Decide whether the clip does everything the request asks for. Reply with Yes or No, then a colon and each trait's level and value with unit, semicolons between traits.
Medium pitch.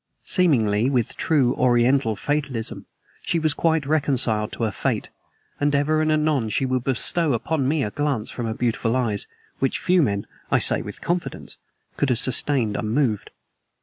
No: low, 130 Hz